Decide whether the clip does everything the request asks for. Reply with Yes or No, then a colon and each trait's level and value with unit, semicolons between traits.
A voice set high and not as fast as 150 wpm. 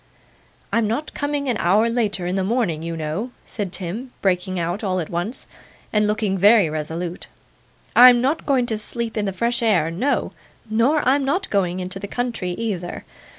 No: high, 210 Hz; average, 180 wpm